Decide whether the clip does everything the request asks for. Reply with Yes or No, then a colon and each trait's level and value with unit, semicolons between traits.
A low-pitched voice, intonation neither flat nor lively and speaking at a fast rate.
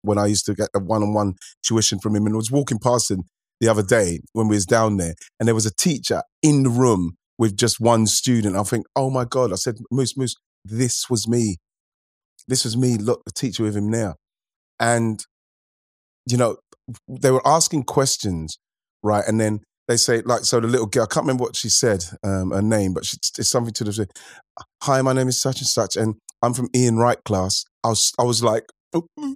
Yes: low, 115 Hz; average, 3.0 semitones; fast, 220 wpm